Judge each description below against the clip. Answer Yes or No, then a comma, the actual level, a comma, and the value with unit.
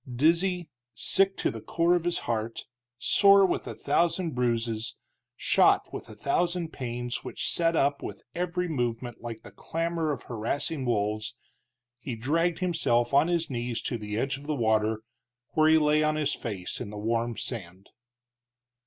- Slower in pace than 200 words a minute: Yes, average, 165 wpm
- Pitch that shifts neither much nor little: No, wide, 6.4 semitones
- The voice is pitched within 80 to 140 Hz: Yes, low, 135 Hz